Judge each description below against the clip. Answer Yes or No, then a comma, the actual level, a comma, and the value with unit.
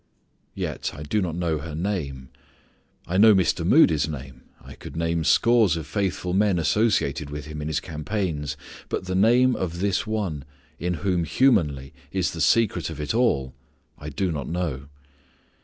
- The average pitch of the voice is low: Yes, very low, 85 Hz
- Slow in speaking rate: No, average, 170 wpm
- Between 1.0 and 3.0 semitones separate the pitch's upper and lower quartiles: No, average, 4.7 semitones